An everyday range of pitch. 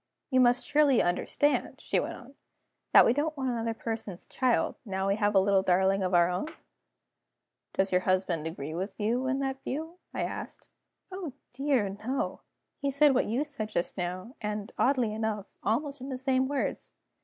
No: wide, 5.7 semitones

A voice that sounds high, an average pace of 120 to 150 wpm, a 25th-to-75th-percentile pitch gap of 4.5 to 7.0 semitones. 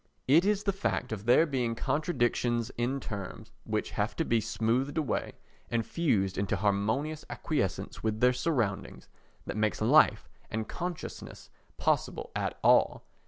No: low, 120 Hz; average, 145 wpm; wide, 5.6 semitones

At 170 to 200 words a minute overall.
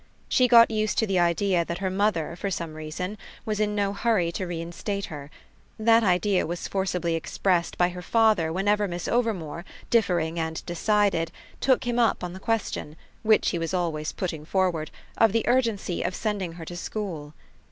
Yes: average, 180 wpm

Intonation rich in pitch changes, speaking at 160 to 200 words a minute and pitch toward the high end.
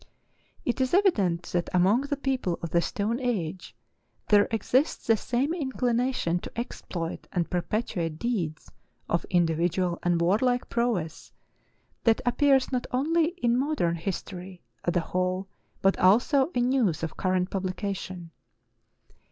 No: wide, 6.0 semitones; slow, 135 wpm; high, 195 Hz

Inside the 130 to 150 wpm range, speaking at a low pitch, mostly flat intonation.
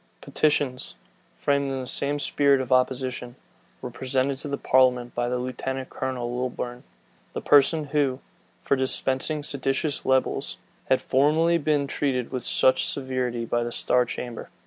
Yes: average, 145 wpm; low, 130 Hz; narrow, 2.0 semitones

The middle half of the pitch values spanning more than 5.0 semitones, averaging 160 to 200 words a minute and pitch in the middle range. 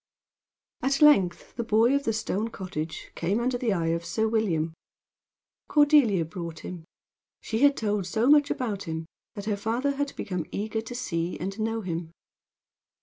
No: wide, 5.6 semitones; average, 165 wpm; high, 215 Hz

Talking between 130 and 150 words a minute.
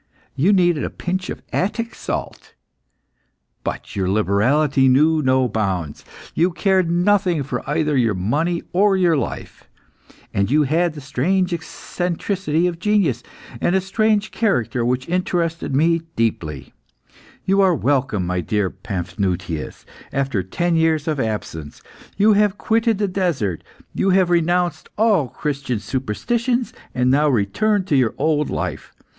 Yes: average, 140 wpm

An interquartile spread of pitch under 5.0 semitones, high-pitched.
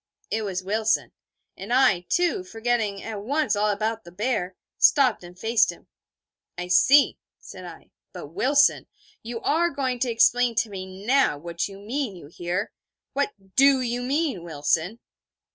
No: wide, 5.6 semitones; high, 220 Hz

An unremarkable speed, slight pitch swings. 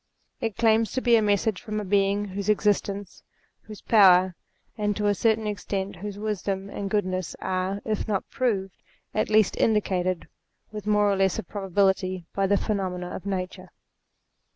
Yes: average, 165 wpm; narrow, 1.9 semitones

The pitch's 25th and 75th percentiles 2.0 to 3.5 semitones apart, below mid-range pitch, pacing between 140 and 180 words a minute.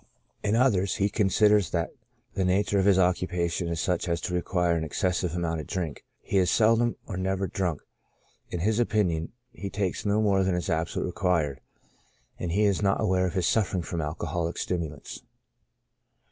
Yes: average, 2.9 semitones; very low, 90 Hz; average, 175 wpm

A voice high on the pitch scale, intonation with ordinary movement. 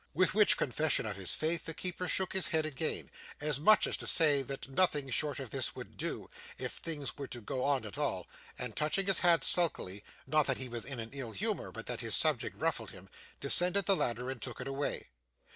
No: medium, 145 Hz; average, 4.8 semitones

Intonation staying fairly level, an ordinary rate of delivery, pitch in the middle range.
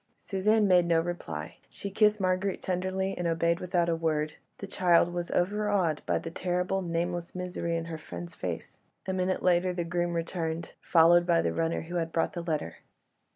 Yes: narrow, 1.9 semitones; average, 185 wpm; medium, 175 Hz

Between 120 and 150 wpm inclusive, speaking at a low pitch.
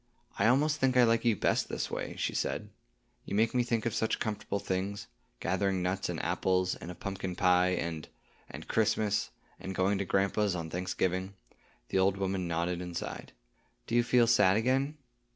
No: average, 170 wpm; low, 100 Hz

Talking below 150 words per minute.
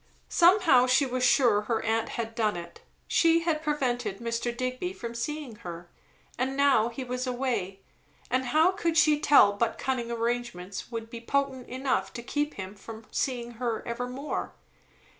No: average, 160 wpm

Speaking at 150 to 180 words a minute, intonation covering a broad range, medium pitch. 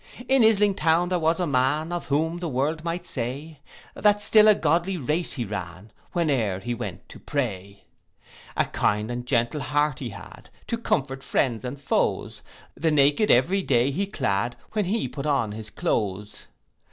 Yes: average, 175 wpm; wide, 6.3 semitones; medium, 145 Hz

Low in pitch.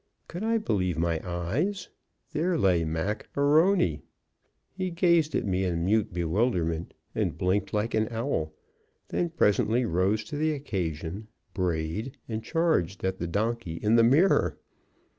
Yes: low, 105 Hz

